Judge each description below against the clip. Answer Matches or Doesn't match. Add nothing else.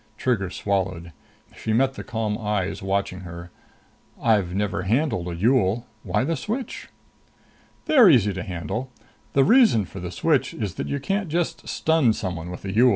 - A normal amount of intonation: Doesn't match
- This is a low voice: Matches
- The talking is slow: Doesn't match